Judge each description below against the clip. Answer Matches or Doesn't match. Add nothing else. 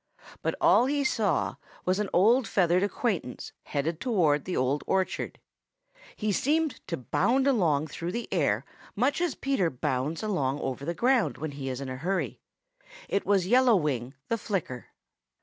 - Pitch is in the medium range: Matches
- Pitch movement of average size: Doesn't match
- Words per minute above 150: Matches